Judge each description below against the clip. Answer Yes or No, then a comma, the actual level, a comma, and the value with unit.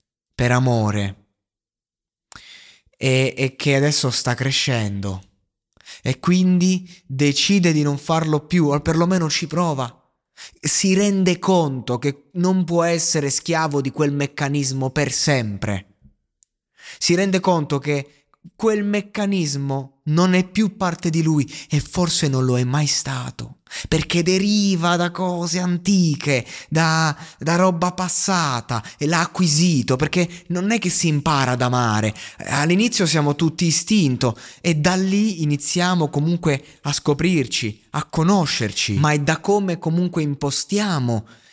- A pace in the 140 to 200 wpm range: No, average, 130 wpm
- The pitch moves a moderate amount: Yes, average, 5.0 semitones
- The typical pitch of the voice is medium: Yes, medium, 155 Hz